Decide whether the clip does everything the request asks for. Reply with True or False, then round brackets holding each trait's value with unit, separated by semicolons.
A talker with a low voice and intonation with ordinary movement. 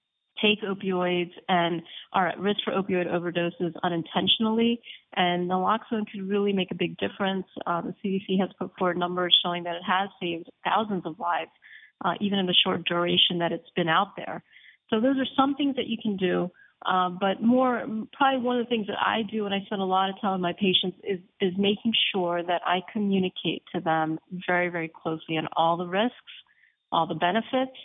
False (190 Hz; 3.3 semitones)